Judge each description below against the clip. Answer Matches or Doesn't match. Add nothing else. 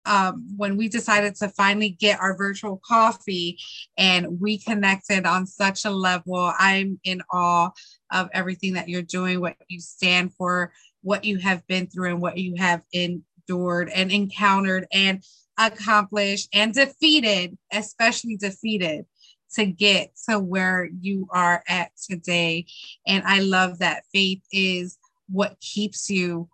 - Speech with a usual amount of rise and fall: Doesn't match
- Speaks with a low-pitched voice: Doesn't match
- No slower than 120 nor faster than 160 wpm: Matches